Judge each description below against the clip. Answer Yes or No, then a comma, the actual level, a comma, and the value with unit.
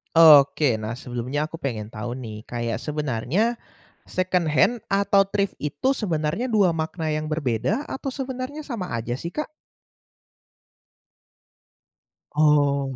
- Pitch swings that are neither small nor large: No, wide, 7.6 semitones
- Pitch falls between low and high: Yes, medium, 155 Hz